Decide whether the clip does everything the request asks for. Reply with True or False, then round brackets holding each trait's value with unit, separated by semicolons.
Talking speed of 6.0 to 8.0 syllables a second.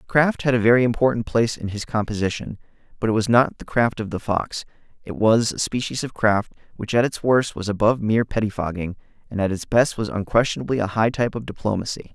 True (6.1 syllables/s)